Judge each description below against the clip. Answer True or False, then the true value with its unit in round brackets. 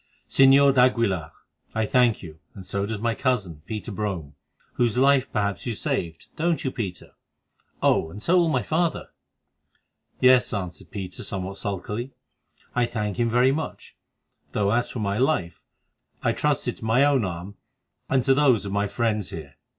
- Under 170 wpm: True (160 wpm)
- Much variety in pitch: False (4.7 semitones)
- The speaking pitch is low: True (110 Hz)